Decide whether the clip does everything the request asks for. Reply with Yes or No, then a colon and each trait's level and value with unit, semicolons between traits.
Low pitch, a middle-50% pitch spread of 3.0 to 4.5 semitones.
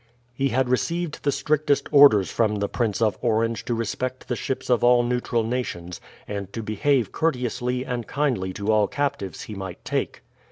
Yes: low, 120 Hz; average, 3.7 semitones